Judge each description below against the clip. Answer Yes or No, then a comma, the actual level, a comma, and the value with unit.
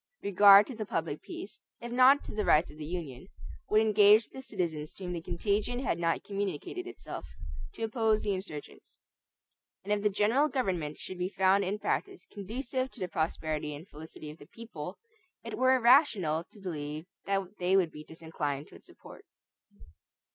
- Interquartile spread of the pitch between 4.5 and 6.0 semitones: Yes, average, 5.3 semitones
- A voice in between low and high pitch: No, high, 195 Hz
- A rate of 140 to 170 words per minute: No, average, 180 wpm